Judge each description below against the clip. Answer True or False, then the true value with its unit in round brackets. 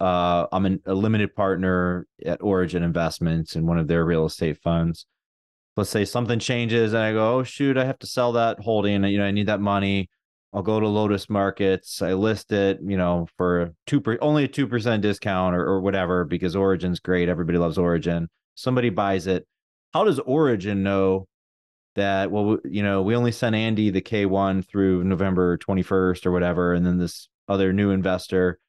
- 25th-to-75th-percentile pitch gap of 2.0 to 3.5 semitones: True (3.0 semitones)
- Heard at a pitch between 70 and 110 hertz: True (95 Hz)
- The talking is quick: False (195 wpm)